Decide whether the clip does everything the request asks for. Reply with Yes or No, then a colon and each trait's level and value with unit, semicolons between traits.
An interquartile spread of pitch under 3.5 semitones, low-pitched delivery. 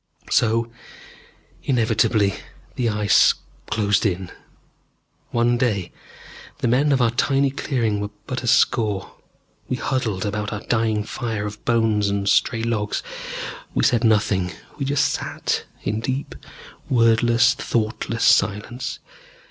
Yes: narrow, 2.5 semitones; low, 115 Hz